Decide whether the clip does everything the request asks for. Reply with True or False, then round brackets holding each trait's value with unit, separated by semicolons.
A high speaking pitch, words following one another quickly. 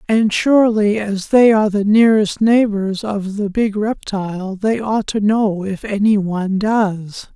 False (210 Hz; 165 wpm)